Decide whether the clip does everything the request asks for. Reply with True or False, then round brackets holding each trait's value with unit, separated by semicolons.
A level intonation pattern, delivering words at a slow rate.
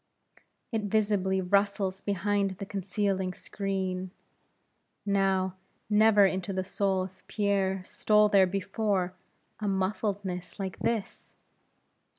True (1.4 semitones; 105 wpm)